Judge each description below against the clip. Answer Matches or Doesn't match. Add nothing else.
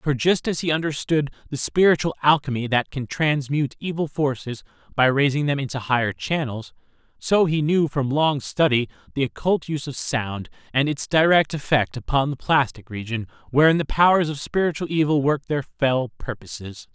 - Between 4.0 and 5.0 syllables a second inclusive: Doesn't match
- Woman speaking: Doesn't match